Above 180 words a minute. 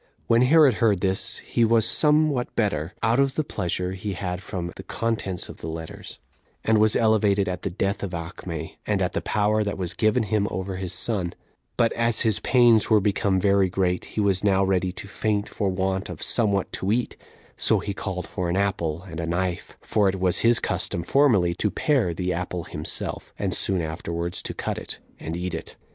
Yes: fast, 205 wpm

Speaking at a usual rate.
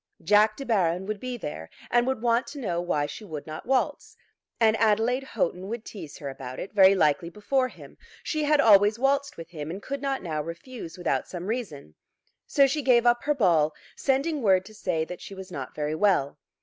No: fast, 210 wpm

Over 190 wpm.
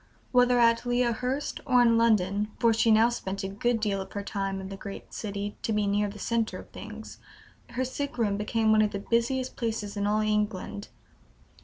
Yes: average, 200 wpm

